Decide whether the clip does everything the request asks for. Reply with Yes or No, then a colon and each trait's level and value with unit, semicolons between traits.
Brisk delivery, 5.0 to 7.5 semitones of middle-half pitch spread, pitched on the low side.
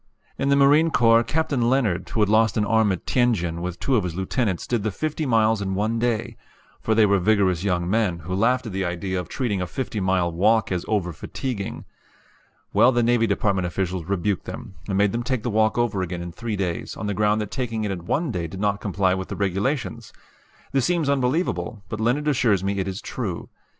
No: fast, 220 wpm; average, 4.2 semitones; low, 105 Hz